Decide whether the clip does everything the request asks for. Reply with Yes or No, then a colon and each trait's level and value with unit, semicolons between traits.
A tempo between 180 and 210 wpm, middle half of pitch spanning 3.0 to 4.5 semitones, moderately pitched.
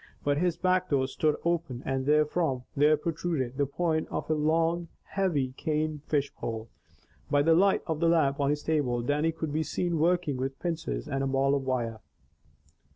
Yes: average, 185 wpm; average, 3.3 semitones; medium, 150 Hz